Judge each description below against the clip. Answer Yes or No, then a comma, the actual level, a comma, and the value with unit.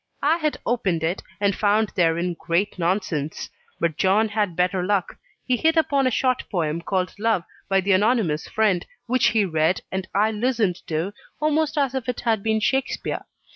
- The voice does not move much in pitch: No, average, 5.2 semitones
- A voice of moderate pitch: No, high, 205 Hz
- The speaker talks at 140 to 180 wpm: Yes, average, 175 wpm